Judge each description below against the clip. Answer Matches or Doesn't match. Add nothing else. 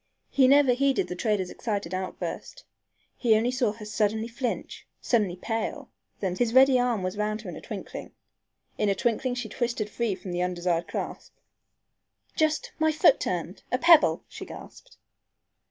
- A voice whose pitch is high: Matches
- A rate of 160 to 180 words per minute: Matches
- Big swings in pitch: Doesn't match